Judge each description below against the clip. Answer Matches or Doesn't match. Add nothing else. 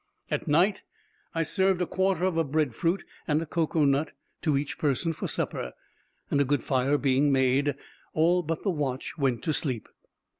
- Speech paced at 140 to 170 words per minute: Doesn't match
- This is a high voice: Doesn't match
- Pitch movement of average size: Matches